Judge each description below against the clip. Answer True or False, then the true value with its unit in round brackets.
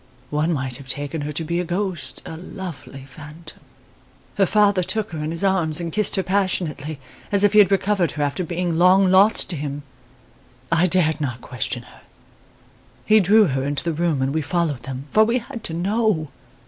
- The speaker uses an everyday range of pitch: True (4.7 semitones)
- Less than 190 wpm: False (200 wpm)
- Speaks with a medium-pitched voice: True (170 Hz)